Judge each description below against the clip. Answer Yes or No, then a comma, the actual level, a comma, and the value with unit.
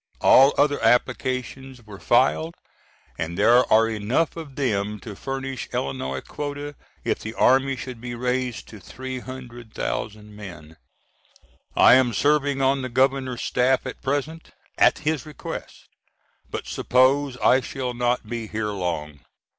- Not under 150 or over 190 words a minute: No, slow, 135 wpm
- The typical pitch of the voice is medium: No, low, 125 Hz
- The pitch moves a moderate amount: Yes, average, 3.9 semitones